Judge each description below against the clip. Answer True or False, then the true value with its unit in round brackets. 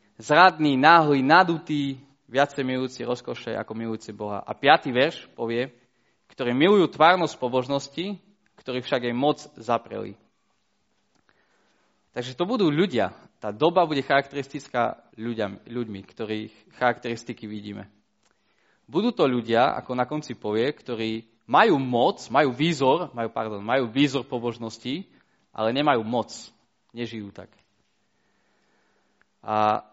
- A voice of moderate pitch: False (120 Hz)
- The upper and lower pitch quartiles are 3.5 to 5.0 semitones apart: True (3.9 semitones)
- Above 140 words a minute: False (115 wpm)